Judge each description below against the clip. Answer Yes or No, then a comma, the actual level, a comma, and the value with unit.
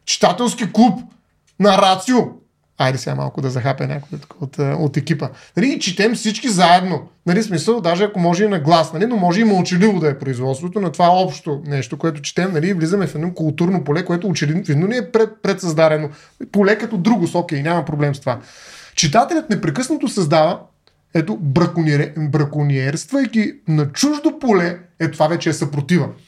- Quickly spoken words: Yes, fast, 170 wpm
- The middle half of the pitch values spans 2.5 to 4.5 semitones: No, average, 5.1 semitones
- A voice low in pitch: No, medium, 175 Hz